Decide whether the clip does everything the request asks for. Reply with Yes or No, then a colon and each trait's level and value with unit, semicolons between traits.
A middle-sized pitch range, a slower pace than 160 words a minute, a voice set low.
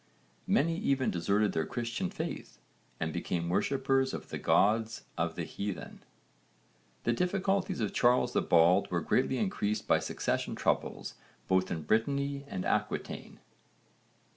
No: wide, 6.7 semitones; slow, 135 wpm; low, 115 Hz